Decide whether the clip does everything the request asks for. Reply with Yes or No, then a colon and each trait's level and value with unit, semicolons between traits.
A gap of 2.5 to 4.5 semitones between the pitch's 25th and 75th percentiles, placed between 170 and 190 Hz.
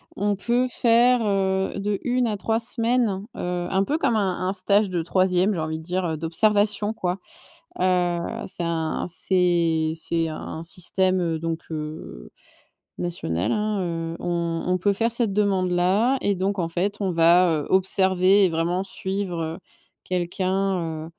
Yes: average, 3.2 semitones; medium, 185 Hz